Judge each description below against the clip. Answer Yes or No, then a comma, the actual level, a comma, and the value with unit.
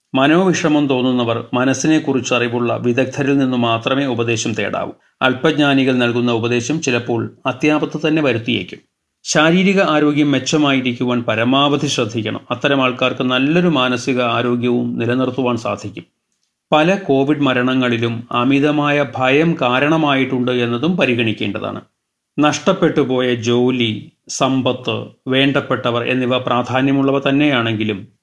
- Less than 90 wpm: No, average, 95 wpm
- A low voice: Yes, low, 130 Hz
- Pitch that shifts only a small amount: No, average, 3.1 semitones